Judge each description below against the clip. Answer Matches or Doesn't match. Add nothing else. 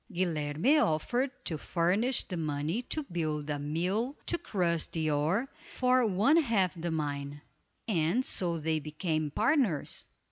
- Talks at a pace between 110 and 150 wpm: Matches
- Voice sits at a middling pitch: Matches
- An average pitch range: Doesn't match